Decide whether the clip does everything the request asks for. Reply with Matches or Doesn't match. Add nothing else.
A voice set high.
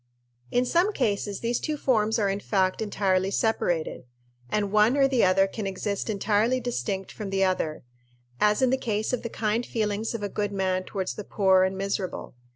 Matches